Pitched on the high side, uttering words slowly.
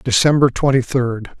No: low, 130 Hz; slow, 130 wpm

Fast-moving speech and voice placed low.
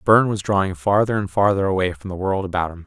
Yes: fast, 250 wpm; very low, 95 Hz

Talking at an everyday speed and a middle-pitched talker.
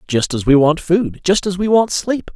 No: fast, 255 wpm; medium, 175 Hz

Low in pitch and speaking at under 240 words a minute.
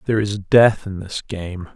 Yes: low, 100 Hz; fast, 205 wpm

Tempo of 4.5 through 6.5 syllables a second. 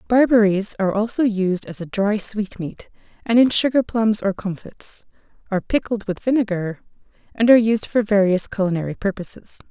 Yes: 5.3 syllables/s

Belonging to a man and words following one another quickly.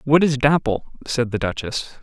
No: male; average, 180 wpm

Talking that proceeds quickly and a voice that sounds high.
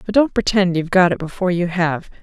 No: fast, 245 wpm; medium, 180 Hz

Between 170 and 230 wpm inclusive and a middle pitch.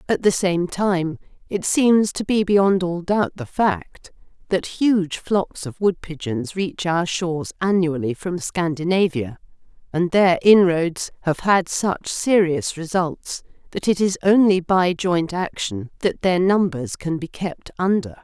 No: average, 150 wpm; medium, 175 Hz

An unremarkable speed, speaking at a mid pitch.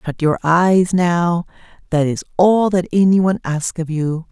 Yes: average, 180 wpm; medium, 170 Hz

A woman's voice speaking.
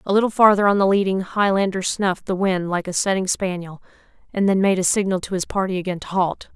Yes: female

